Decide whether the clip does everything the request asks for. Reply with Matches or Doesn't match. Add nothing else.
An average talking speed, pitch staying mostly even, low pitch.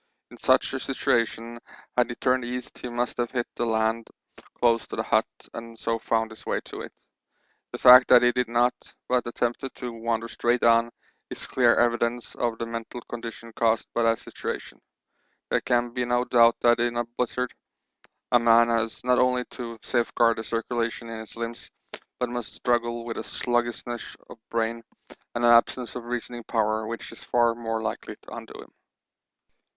Matches